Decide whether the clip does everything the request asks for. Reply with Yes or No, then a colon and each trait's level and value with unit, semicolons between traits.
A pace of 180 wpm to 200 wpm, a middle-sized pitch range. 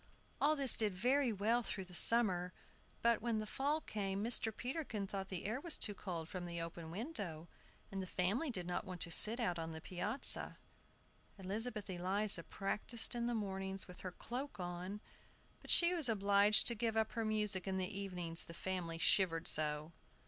Yes: average, 185 wpm; average, 4.2 semitones